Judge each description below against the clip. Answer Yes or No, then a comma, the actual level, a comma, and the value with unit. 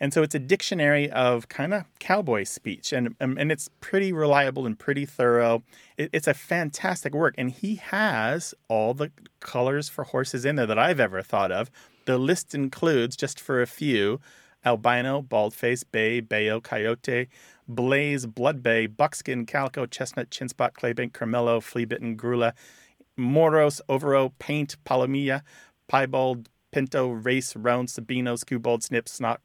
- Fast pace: No, average, 155 wpm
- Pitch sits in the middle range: No, low, 130 Hz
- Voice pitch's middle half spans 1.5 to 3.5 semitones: Yes, average, 3.1 semitones